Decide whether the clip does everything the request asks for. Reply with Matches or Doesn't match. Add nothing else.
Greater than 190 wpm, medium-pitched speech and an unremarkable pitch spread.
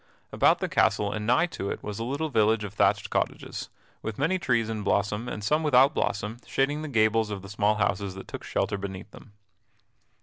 Doesn't match